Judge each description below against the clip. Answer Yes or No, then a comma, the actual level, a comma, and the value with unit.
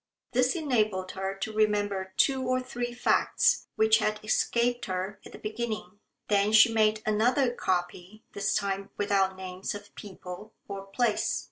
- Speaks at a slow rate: No, average, 150 wpm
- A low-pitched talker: No, high, 210 Hz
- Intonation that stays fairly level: No, average, 3.3 semitones